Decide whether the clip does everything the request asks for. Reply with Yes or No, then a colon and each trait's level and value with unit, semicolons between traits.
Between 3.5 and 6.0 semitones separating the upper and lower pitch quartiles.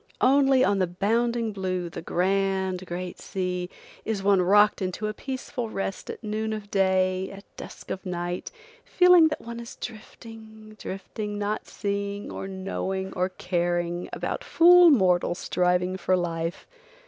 No: average, 3.1 semitones